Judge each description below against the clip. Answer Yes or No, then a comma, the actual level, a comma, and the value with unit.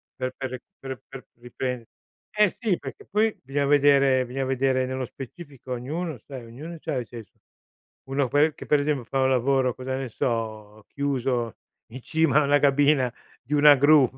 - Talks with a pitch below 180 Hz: Yes, low, 135 Hz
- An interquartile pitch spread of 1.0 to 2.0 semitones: No, narrow, 2.4 semitones